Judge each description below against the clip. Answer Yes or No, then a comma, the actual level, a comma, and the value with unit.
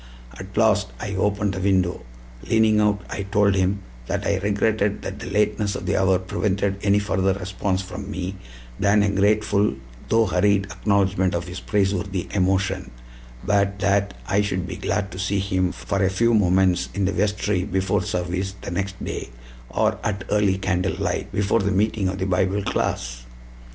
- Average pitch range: No, narrow, 1.6 semitones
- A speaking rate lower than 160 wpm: No, average, 170 wpm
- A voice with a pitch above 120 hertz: No, low, 100 Hz